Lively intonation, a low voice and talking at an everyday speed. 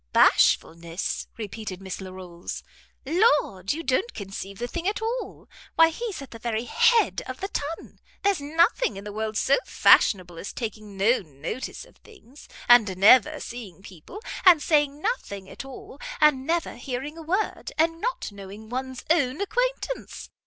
No: wide, 8.7 semitones; very high, 255 Hz; average, 160 wpm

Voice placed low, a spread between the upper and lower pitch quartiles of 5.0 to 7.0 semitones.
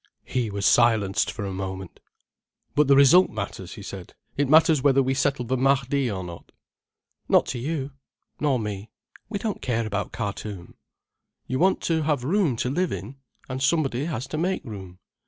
Yes: low, 130 Hz; average, 5.3 semitones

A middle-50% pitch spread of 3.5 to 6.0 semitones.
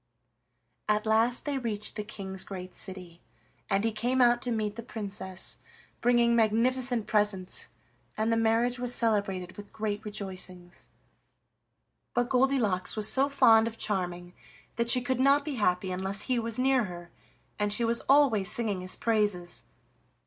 Yes: average, 3.8 semitones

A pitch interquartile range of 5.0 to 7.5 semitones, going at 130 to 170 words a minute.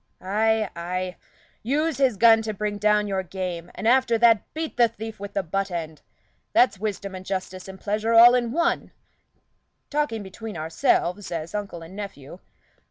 No: average, 3.5 semitones; average, 165 wpm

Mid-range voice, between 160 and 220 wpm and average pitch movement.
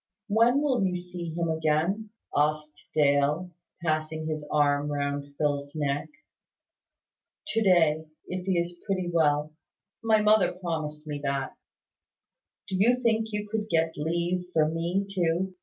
No: medium, 165 Hz; average, 140 wpm; average, 4.0 semitones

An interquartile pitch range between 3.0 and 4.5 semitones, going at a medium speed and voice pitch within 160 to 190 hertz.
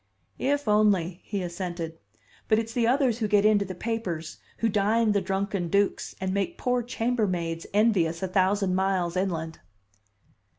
No: average, 3.5 semitones; average, 155 wpm; high, 200 Hz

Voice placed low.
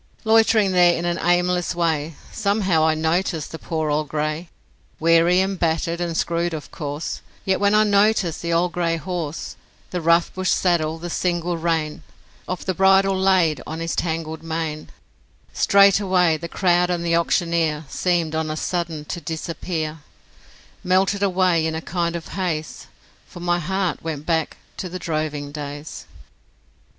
No: medium, 170 Hz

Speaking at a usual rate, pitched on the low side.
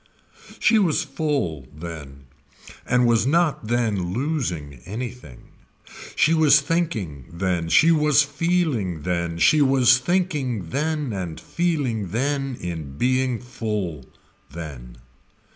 No: slow, 110 wpm; low, 120 Hz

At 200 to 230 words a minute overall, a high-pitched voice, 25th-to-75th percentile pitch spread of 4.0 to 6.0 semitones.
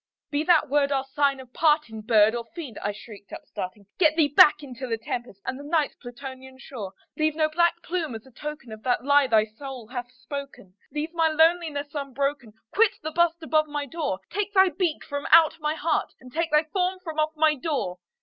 Yes: fast, 205 wpm; very high, 290 Hz; average, 4.3 semitones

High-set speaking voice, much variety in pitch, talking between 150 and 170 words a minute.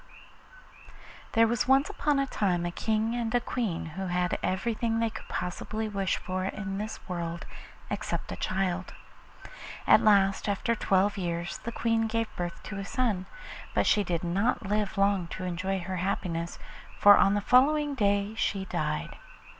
No: high, 200 Hz; average, 3.4 semitones; average, 160 wpm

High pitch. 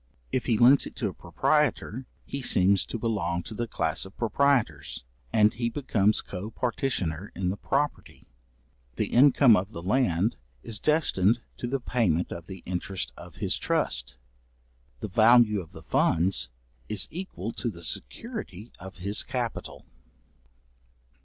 No: low, 105 Hz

